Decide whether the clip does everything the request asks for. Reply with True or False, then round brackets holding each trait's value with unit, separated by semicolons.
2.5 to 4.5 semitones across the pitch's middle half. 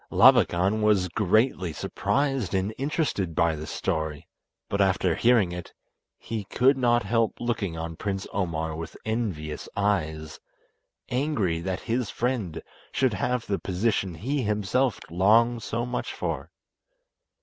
False (5.5 semitones)